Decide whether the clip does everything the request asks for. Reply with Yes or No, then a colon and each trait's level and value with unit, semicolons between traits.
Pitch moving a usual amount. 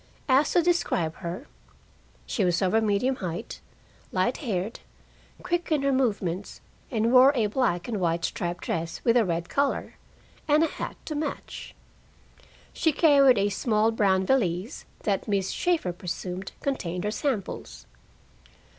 No: wide, 6.8 semitones